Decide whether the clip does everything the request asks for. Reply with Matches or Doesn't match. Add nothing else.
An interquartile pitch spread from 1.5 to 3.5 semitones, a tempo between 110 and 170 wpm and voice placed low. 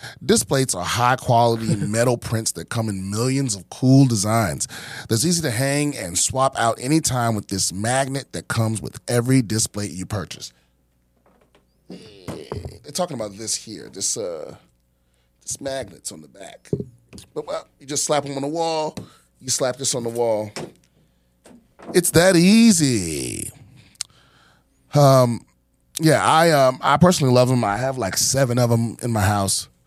Doesn't match